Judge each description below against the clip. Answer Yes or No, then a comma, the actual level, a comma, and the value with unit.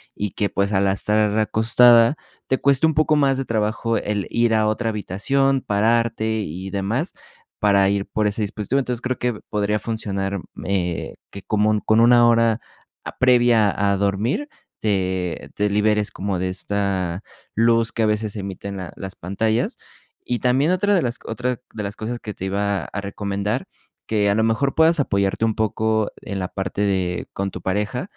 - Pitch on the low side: Yes, low, 105 Hz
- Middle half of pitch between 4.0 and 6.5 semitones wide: No, average, 2.9 semitones